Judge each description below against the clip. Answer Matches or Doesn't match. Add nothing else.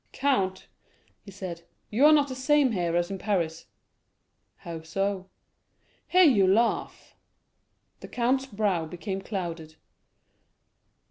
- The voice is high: Matches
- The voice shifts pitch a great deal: Matches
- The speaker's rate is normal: Doesn't match